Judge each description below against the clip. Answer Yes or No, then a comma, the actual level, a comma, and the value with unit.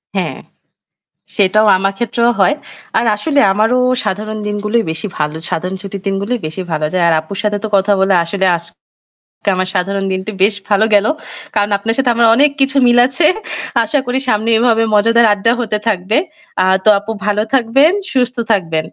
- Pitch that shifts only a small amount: No, average, 3.4 semitones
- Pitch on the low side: No, high, 210 Hz